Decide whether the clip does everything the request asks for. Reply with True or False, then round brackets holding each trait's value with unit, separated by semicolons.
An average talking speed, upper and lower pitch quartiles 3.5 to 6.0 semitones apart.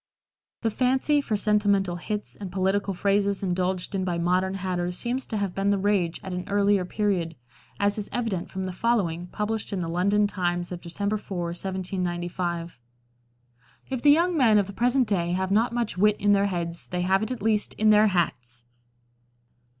False (185 wpm; 2.9 semitones)